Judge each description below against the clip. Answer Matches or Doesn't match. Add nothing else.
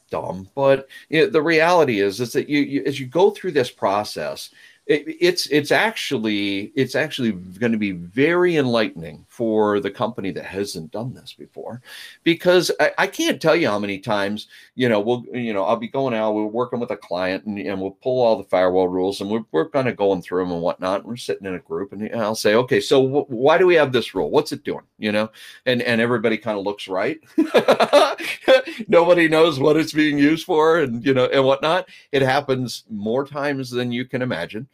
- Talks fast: Matches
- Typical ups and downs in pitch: Doesn't match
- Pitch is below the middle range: Matches